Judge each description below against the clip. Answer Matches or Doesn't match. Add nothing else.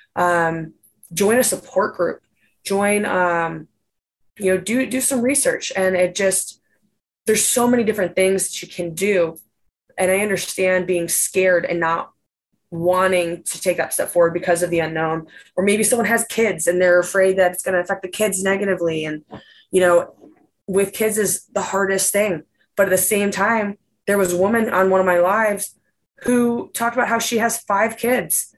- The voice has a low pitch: Doesn't match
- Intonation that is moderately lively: Matches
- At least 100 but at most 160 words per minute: Doesn't match